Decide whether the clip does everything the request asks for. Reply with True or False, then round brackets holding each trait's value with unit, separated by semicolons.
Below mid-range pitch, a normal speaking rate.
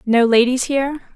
False (255 Hz; 155 wpm)